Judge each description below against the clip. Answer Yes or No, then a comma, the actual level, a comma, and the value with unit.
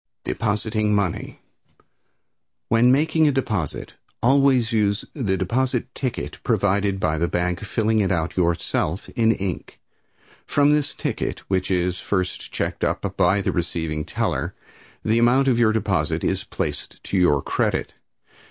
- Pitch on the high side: No, low, 105 Hz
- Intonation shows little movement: No, average, 4.9 semitones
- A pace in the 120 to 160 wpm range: Yes, average, 140 wpm